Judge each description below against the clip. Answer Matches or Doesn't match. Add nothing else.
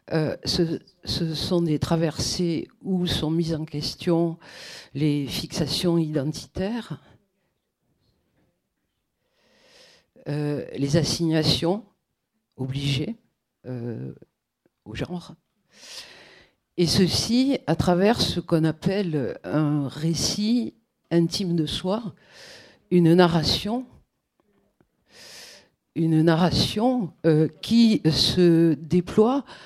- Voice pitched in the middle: Matches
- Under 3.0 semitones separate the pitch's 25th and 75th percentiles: Doesn't match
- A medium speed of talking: Doesn't match